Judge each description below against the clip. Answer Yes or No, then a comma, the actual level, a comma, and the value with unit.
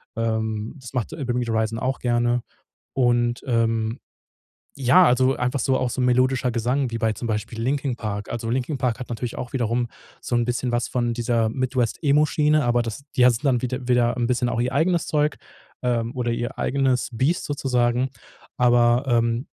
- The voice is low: Yes, low, 120 Hz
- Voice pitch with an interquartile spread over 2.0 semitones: No, narrow, 1.7 semitones